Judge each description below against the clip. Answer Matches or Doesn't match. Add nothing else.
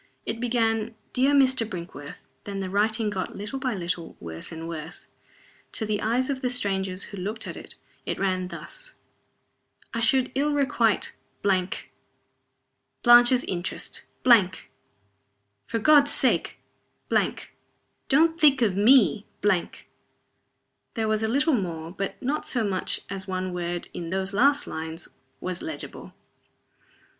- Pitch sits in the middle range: Doesn't match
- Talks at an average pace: Doesn't match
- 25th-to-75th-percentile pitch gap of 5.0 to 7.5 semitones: Matches